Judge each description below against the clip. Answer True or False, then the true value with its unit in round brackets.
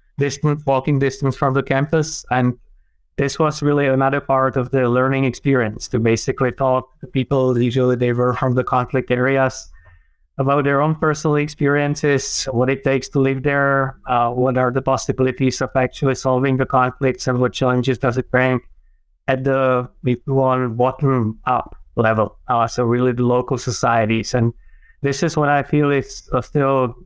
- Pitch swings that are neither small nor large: False (1.7 semitones)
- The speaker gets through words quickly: False (165 wpm)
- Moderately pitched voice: False (130 Hz)